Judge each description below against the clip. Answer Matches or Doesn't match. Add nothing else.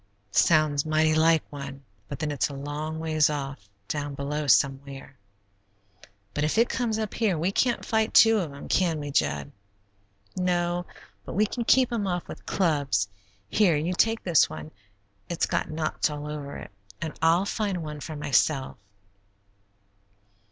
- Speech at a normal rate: Matches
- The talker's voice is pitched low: Doesn't match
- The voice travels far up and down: Doesn't match